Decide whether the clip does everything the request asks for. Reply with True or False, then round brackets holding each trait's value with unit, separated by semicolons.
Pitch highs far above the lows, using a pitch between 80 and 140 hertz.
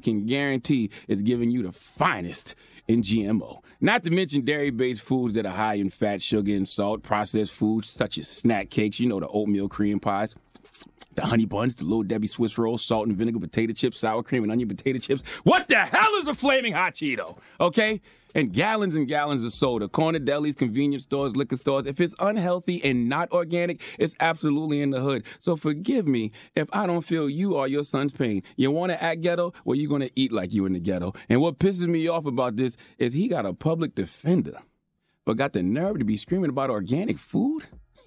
True (6.8 semitones; 135 Hz)